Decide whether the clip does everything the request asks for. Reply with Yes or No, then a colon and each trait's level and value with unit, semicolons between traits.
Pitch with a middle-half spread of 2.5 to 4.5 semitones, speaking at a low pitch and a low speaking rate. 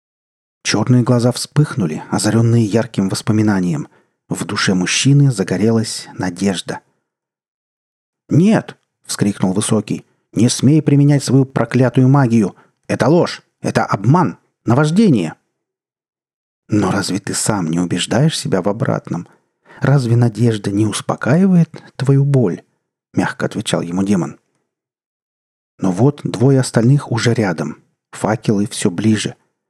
No: average, 5.1 semitones; low, 115 Hz; slow, 105 wpm